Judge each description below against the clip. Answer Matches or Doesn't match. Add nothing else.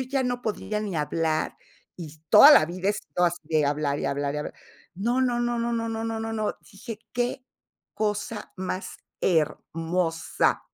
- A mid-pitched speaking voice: Doesn't match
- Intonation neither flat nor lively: Doesn't match